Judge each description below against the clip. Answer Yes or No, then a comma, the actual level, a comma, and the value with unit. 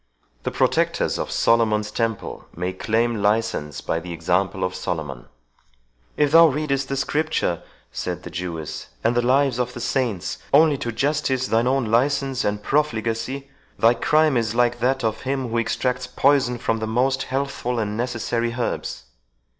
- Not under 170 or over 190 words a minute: No, average, 160 wpm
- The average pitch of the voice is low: Yes, low, 120 Hz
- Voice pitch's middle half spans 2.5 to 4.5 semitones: Yes, average, 3.9 semitones